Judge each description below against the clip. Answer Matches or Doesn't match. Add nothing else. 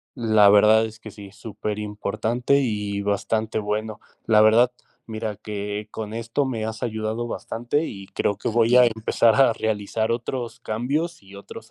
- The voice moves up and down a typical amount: Doesn't match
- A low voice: Matches